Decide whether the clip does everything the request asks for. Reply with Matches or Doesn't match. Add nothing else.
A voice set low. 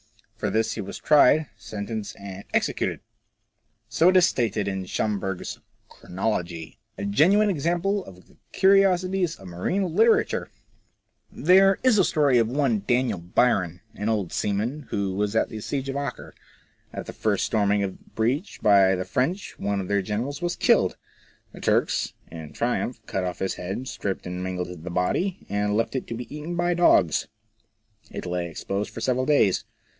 Matches